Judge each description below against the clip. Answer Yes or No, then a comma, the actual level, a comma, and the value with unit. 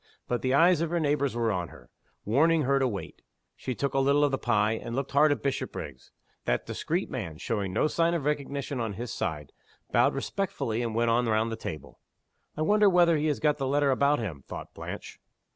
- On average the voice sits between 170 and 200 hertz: No, low, 135 Hz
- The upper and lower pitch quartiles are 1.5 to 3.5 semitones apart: No, average, 4.9 semitones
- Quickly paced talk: Yes, fast, 215 wpm